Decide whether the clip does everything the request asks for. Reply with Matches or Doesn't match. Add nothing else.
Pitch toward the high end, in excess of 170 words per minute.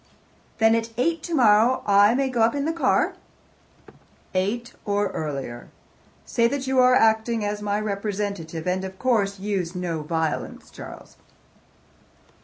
Doesn't match